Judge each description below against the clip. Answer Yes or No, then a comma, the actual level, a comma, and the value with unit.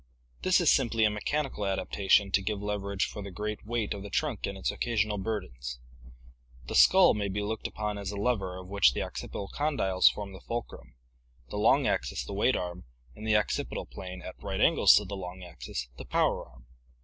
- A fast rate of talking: Yes, fast, 210 wpm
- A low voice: Yes, low, 100 Hz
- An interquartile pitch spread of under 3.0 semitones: Yes, narrow, 2.6 semitones